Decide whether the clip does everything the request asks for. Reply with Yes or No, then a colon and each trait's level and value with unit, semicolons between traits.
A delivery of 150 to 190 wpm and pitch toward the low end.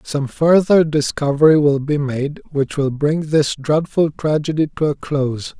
No: average, 160 wpm; medium, 150 Hz